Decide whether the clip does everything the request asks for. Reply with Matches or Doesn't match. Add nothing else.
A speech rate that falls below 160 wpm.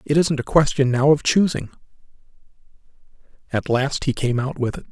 Doesn't match